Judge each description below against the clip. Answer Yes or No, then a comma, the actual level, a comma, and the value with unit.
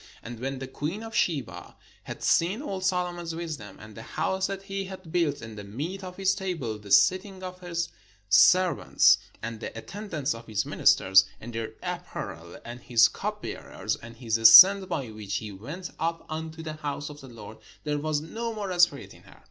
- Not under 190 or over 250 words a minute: Yes, average, 195 wpm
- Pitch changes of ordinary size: No, wide, 8.3 semitones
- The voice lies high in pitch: No, medium, 155 Hz